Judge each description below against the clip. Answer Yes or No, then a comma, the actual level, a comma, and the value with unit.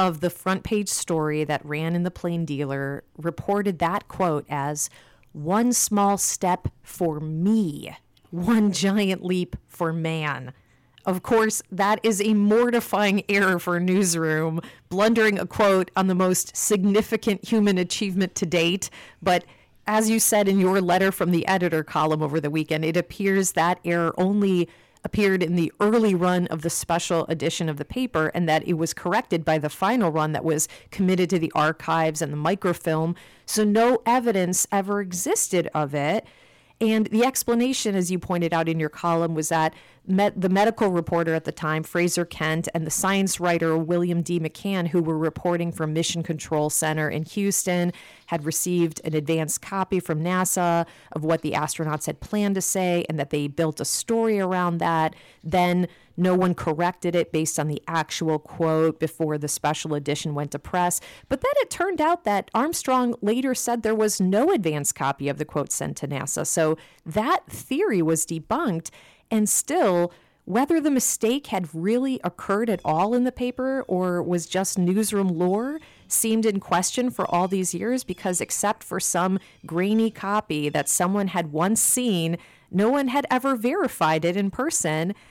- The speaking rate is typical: Yes, average, 175 wpm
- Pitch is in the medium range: Yes, medium, 180 Hz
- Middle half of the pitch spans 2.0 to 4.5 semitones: Yes, average, 4.1 semitones